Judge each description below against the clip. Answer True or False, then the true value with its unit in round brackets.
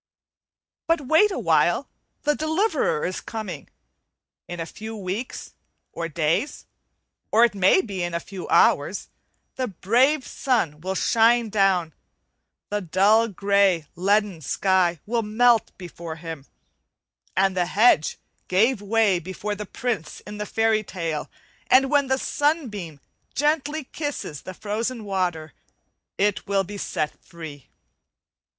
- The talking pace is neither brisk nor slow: False (130 wpm)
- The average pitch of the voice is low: False (205 Hz)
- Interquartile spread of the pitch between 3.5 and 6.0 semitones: True (5.1 semitones)